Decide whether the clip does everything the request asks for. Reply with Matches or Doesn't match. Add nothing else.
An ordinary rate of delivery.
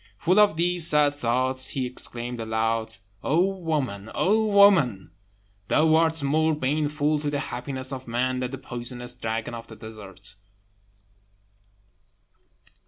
Doesn't match